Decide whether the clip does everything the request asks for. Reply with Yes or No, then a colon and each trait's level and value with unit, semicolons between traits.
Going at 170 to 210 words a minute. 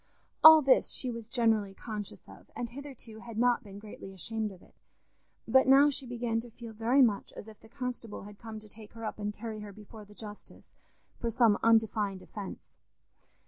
Yes: average, 195 wpm